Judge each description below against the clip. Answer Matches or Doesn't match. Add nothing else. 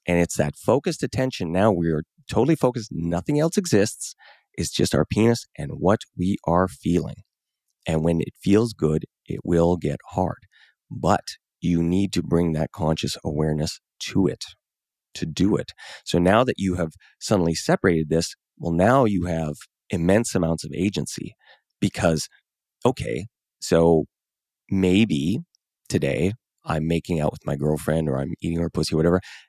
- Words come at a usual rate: Matches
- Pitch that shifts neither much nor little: Matches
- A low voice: Matches